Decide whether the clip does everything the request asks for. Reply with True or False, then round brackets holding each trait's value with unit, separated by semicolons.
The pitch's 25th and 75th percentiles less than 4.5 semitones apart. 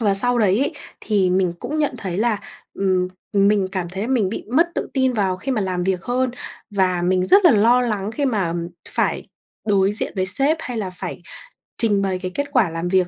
False (4.8 semitones)